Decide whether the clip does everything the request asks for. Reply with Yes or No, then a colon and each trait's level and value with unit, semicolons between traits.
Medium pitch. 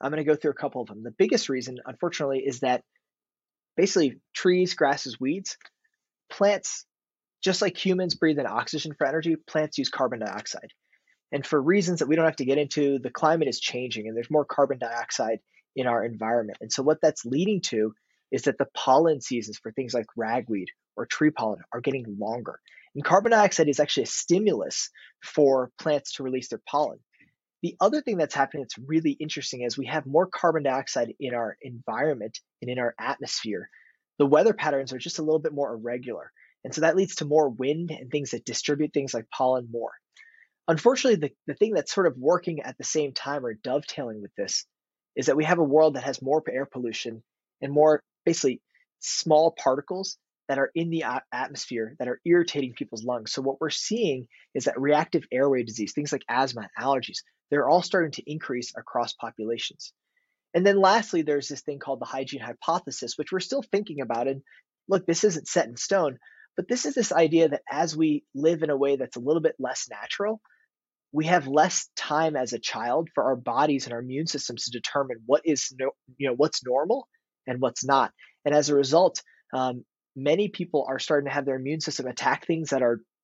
Yes: medium, 145 Hz